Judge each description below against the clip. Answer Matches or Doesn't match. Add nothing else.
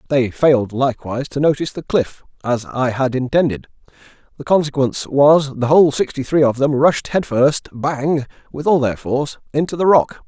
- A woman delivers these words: Doesn't match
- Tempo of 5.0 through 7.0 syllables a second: Matches